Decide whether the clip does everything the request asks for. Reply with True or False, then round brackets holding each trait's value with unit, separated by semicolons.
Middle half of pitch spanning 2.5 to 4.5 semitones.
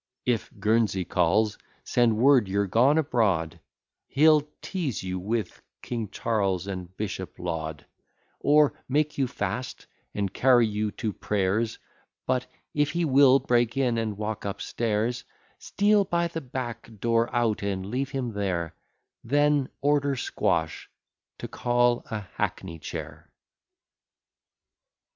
False (4.9 semitones)